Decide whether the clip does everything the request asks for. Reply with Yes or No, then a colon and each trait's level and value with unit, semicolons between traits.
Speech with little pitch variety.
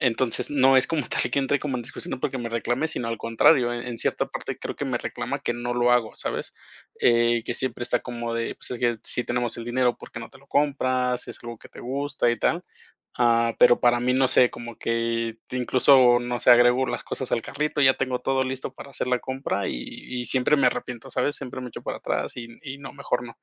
Yes: narrow, 1.8 semitones